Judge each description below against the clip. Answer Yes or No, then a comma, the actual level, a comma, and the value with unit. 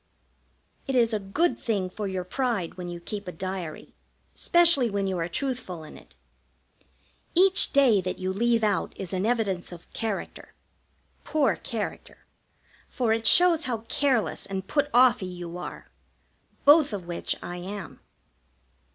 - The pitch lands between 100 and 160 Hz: No, high, 210 Hz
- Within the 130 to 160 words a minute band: Yes, average, 155 wpm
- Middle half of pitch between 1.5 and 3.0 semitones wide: No, wide, 5.6 semitones